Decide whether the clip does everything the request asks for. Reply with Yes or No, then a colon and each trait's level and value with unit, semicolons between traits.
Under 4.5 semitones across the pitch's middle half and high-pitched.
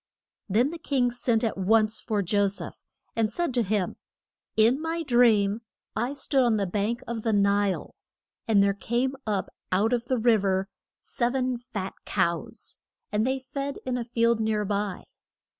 Yes: average, 3.4 semitones; high, 225 Hz